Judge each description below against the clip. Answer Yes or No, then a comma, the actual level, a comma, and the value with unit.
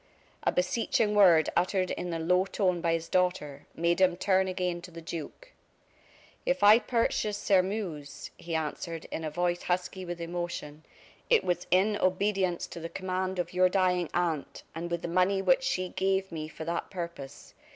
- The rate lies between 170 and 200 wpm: Yes, average, 175 wpm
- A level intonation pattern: Yes, narrow, 2.0 semitones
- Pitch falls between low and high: Yes, medium, 180 Hz